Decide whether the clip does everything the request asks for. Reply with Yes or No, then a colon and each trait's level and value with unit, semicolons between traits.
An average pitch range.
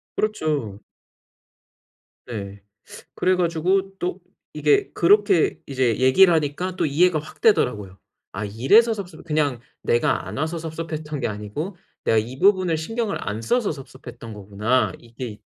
No: wide, 7.5 semitones